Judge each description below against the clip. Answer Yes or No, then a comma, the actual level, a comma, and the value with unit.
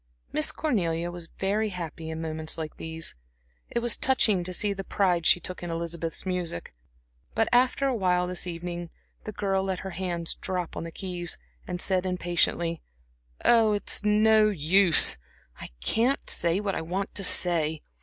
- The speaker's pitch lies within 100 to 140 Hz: No, medium, 180 Hz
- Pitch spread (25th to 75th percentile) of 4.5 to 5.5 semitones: No, average, 3.1 semitones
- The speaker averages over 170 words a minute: No, average, 165 wpm